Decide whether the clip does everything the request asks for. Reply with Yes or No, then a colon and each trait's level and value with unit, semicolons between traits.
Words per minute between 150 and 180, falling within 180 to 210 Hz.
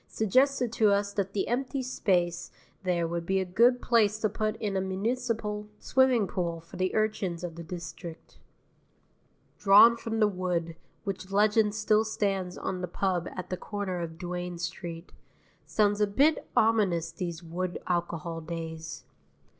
Yes: average, 155 wpm; high, 190 Hz